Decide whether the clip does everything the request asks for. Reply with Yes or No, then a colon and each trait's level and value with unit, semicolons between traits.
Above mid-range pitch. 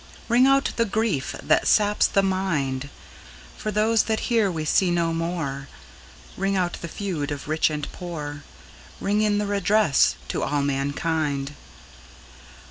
No: medium, 175 Hz